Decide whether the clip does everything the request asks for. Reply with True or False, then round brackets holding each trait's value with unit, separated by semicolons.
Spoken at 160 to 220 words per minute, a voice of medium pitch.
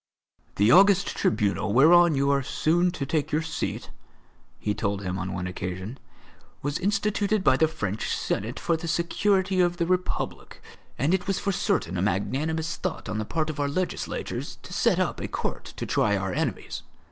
True (180 wpm; 155 Hz)